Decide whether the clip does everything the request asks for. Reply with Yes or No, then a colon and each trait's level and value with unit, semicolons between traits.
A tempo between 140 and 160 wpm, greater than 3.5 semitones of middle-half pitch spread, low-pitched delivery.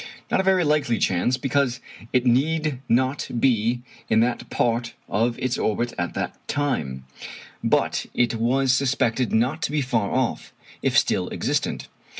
No: average, 150 wpm; average, 3.0 semitones; low, 125 Hz